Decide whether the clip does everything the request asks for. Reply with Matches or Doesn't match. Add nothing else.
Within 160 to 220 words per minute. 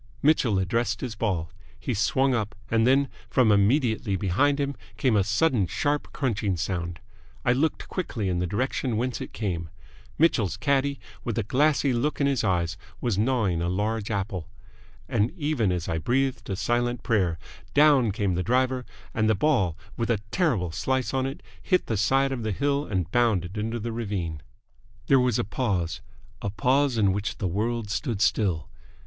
Matches